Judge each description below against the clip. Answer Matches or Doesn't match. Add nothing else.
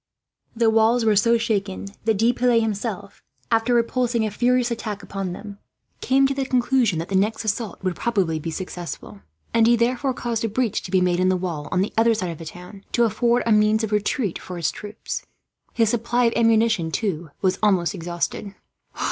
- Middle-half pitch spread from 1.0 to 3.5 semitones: Doesn't match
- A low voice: Doesn't match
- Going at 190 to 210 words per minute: Matches